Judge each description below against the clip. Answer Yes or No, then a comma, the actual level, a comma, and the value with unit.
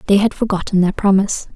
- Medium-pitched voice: No, high, 195 Hz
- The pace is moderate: Yes, average, 195 wpm